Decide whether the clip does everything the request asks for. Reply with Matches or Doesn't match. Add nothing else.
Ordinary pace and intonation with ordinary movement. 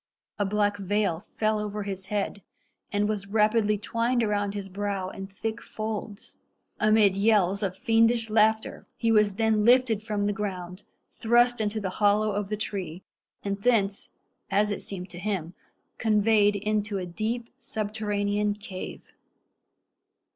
Doesn't match